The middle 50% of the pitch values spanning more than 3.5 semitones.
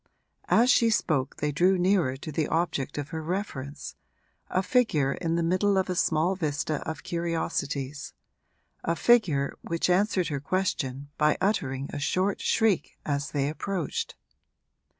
Yes: average, 4.6 semitones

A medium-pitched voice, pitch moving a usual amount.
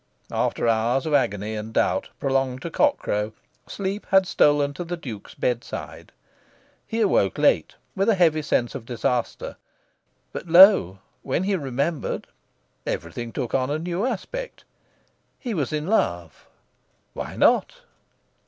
No: medium, 145 Hz; wide, 7.8 semitones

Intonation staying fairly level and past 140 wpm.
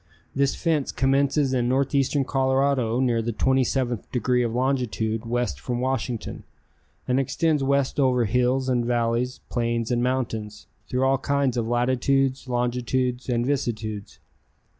No: narrow, 2.0 semitones; slow, 135 wpm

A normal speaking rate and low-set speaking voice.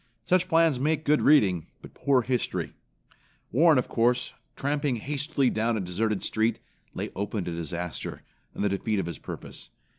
Yes: average, 160 wpm; low, 120 Hz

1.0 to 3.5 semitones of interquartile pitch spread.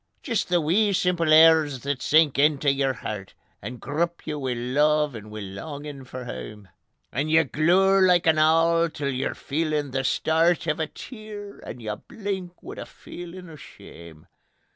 No: average, 4.3 semitones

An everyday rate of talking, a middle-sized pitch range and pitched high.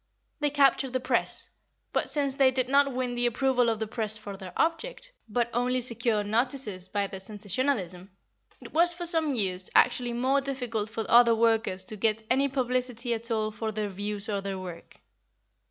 Yes: average, 185 wpm; average, 4.0 semitones; high, 235 Hz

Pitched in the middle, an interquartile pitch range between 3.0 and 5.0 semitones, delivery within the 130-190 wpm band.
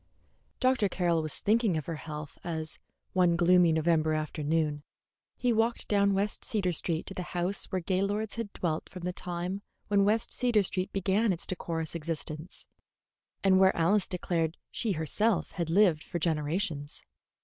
Yes: medium, 180 Hz; average, 3.8 semitones; average, 160 wpm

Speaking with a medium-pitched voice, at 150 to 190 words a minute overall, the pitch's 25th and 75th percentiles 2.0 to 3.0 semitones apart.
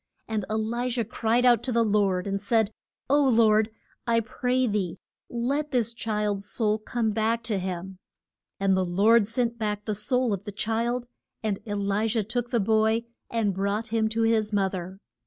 No: high, 220 Hz; average, 185 wpm; narrow, 2.4 semitones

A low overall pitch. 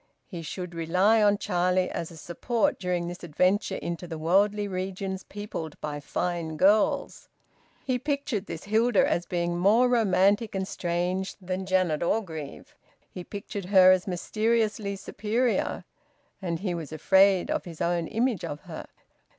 No: medium, 185 Hz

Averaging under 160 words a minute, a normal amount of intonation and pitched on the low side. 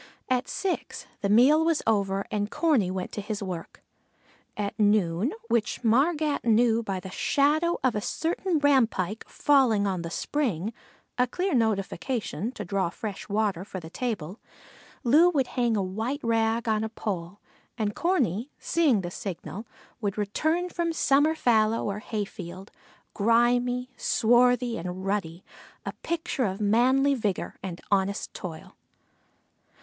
No: average, 145 wpm; average, 4.9 semitones; high, 220 Hz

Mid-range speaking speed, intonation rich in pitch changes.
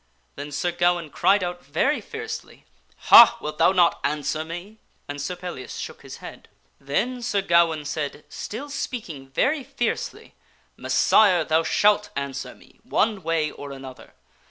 Yes: average, 155 wpm; wide, 5.9 semitones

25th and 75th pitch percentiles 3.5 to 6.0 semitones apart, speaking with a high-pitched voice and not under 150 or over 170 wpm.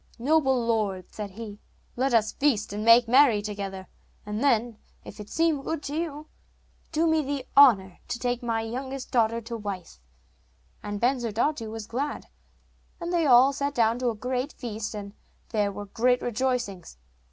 Yes: average, 4.4 semitones; high, 235 Hz; average, 165 wpm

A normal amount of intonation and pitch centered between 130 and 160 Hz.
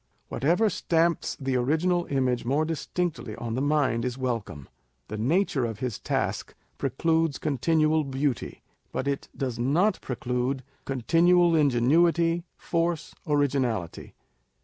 Yes: average, 4.8 semitones; medium, 140 Hz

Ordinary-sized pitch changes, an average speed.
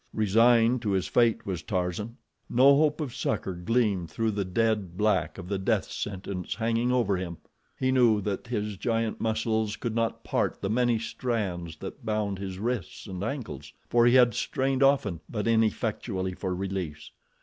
Yes: average, 3.8 semitones; average, 170 wpm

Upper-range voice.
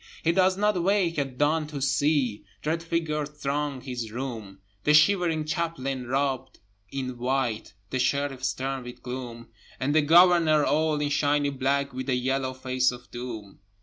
No: medium, 140 Hz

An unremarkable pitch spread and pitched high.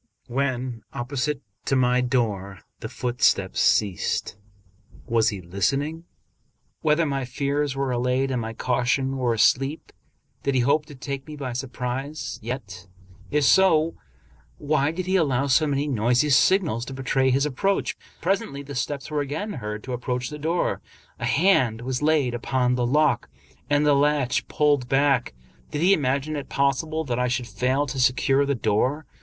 No: average, 3.1 semitones; low, 135 Hz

